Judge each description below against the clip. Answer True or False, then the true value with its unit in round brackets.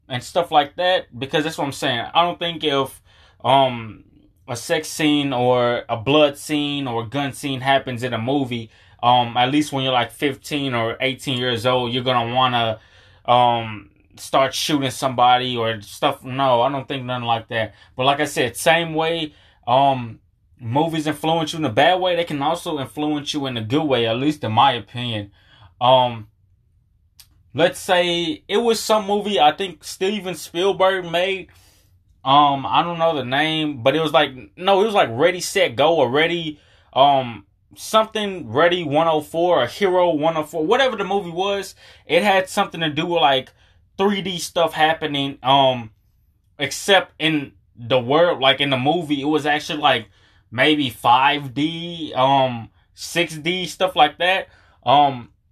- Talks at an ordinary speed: True (170 wpm)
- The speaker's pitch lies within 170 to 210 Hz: False (140 Hz)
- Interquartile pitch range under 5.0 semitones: False (5.6 semitones)